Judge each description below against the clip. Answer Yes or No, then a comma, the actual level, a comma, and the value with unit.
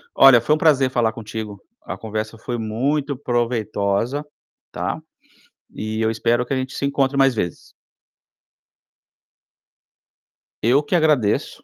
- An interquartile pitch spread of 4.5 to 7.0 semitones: No, average, 3.8 semitones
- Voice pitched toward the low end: Yes, low, 120 Hz